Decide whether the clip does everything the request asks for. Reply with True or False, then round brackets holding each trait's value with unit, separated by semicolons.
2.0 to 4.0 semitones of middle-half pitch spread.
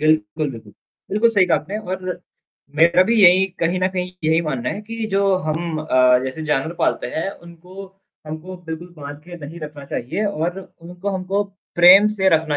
True (3.4 semitones)